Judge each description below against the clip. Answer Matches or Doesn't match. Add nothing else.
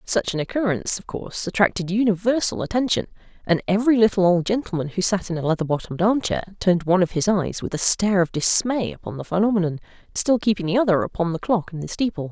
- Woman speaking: Matches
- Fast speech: Matches